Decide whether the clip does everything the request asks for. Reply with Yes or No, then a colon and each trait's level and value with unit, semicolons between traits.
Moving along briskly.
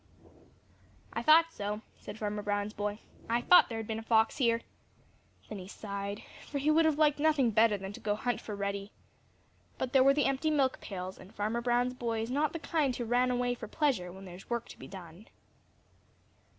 Yes: fast, 210 wpm